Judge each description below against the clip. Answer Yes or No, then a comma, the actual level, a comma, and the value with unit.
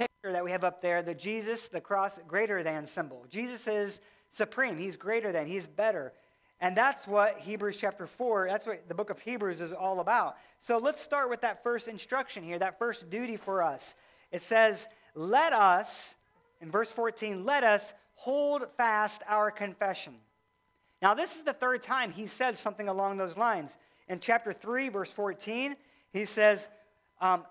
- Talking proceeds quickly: No, average, 175 wpm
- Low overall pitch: No, high, 210 Hz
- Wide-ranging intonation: No, average, 3.5 semitones